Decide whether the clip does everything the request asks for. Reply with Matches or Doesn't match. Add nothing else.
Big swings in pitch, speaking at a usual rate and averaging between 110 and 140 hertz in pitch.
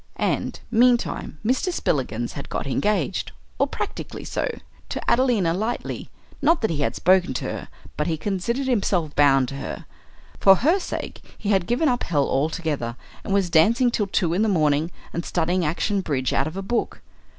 Doesn't match